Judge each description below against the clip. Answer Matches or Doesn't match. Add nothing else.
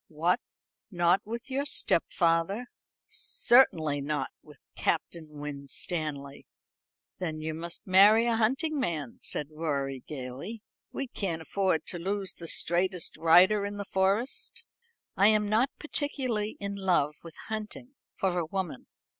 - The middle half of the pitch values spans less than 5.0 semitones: Doesn't match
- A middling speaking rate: Doesn't match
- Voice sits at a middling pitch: Matches